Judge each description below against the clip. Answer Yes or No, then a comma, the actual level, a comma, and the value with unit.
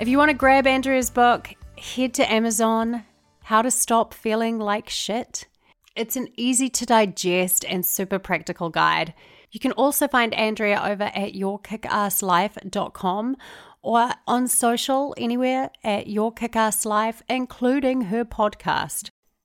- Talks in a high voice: Yes, high, 225 Hz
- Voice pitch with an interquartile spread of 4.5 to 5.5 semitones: No, average, 3.4 semitones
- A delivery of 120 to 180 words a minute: Yes, slow, 135 wpm